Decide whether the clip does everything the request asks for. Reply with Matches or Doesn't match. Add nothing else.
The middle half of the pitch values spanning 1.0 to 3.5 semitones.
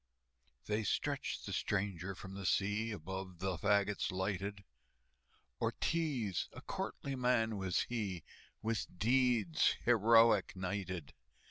Matches